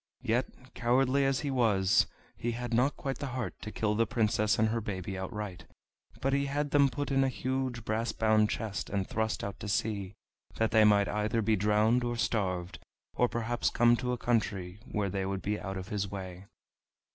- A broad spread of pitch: No, average, 3.3 semitones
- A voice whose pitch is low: Yes, low, 110 Hz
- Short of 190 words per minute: No, average, 200 wpm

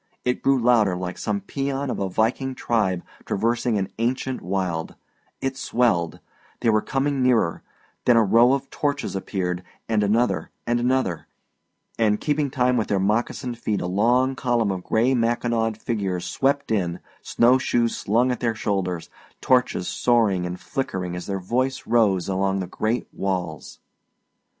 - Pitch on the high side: No, low, 115 Hz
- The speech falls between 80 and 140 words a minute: No, average, 155 wpm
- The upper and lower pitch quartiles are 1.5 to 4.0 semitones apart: No, average, 4.6 semitones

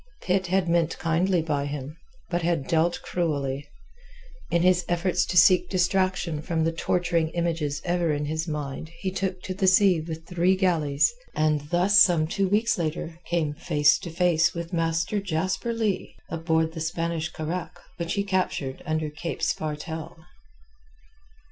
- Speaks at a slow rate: No, average, 155 wpm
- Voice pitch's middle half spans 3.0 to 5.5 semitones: No, narrow, 2.4 semitones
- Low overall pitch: No, medium, 170 Hz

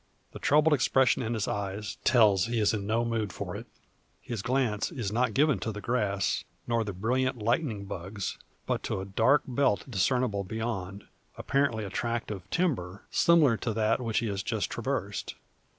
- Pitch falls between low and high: No, low, 110 Hz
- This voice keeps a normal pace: Yes, average, 175 wpm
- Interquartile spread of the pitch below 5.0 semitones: Yes, average, 3.9 semitones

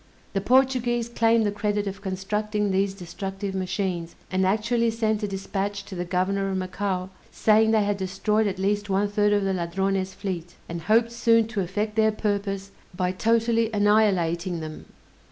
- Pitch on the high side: Yes, high, 200 Hz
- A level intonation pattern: Yes, narrow, 2.3 semitones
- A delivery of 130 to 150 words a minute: No, average, 170 wpm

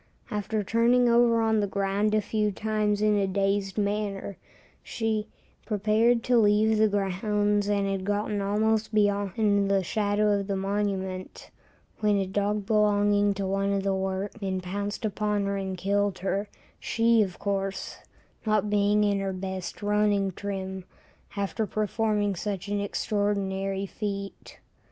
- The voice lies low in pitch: No, high, 205 Hz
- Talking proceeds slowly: No, average, 145 wpm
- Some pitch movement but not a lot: No, narrow, 1.3 semitones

